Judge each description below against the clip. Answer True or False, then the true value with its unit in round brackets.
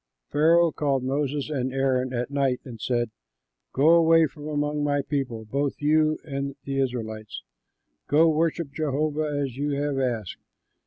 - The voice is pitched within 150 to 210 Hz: False (140 Hz)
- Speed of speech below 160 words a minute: True (150 wpm)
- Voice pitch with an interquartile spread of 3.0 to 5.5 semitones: False (2.6 semitones)